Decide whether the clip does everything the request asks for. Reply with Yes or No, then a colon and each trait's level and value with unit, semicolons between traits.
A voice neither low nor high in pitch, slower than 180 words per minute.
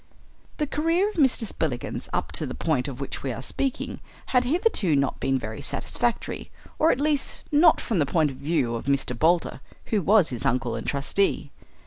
No: medium, 165 Hz; average, 190 wpm